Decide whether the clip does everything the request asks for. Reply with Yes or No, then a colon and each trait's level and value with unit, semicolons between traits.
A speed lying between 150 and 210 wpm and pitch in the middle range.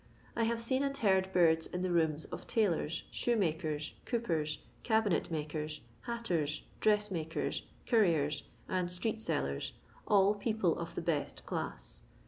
No: slow, 135 wpm; medium, 180 Hz